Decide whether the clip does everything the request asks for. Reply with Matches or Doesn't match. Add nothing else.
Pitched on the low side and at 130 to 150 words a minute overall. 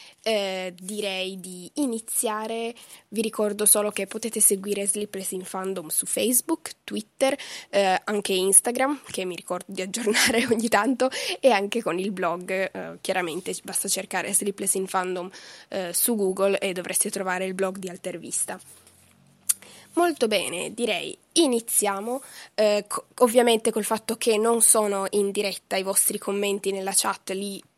Doesn't match